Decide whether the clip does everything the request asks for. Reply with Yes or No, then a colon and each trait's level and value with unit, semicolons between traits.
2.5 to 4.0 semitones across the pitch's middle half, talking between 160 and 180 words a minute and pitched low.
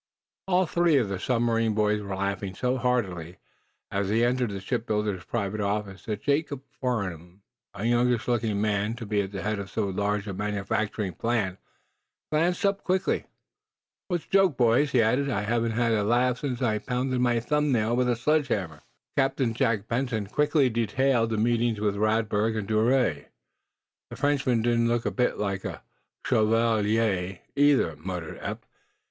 Yes: average, 3.5 semitones; average, 165 wpm; low, 115 Hz